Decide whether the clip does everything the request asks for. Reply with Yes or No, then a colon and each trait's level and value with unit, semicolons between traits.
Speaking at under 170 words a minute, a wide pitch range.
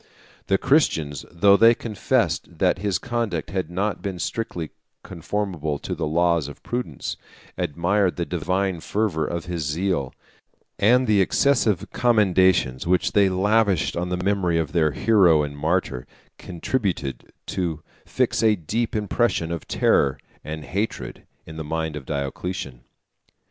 No: average, 140 wpm; average, 4.5 semitones